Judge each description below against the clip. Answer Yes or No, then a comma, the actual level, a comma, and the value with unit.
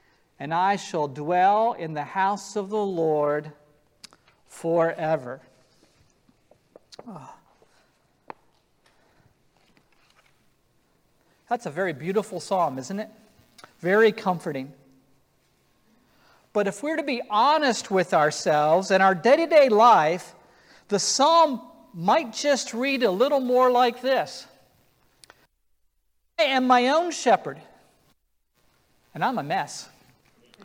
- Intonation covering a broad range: Yes, wide, 8.5 semitones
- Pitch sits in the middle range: No, high, 195 Hz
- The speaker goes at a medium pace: No, slow, 100 wpm